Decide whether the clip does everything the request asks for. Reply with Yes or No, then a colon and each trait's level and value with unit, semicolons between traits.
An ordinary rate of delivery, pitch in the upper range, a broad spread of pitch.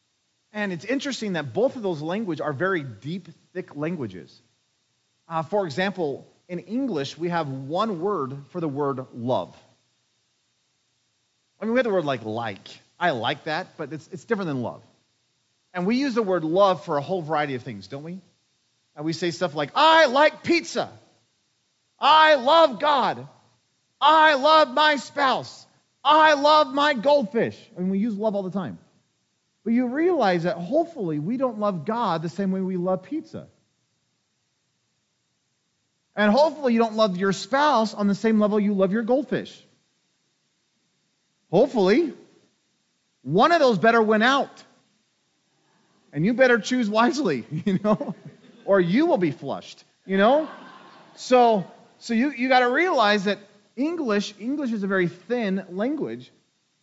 Yes: average, 160 wpm; high, 205 Hz; wide, 7.4 semitones